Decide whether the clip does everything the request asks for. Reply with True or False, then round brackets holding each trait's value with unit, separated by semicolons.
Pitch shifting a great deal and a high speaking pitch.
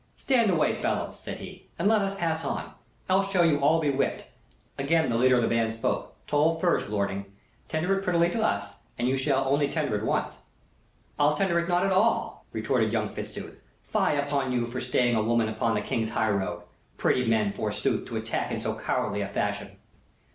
False (6.9 semitones; 140 Hz)